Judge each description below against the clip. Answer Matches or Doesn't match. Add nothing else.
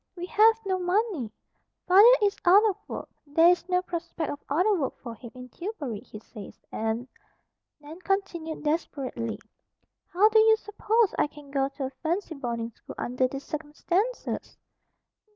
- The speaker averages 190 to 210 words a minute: Doesn't match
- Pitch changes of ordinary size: Doesn't match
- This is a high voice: Matches